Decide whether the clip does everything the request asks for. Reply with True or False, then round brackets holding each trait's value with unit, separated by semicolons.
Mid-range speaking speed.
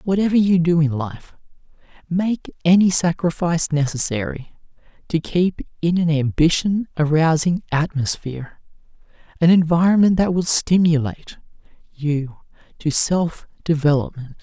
False (105 wpm)